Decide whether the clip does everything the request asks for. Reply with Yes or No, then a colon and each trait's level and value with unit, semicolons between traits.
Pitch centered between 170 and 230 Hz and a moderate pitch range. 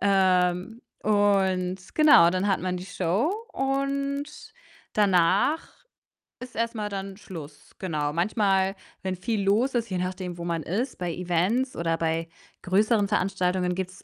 Yes: high, 190 Hz; average, 3.2 semitones